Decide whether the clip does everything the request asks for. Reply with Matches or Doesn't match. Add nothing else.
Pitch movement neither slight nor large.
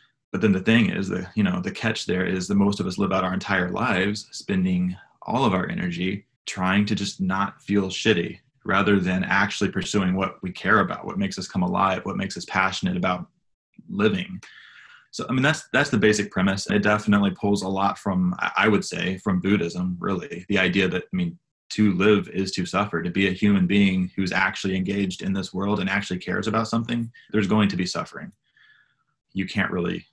Doesn't match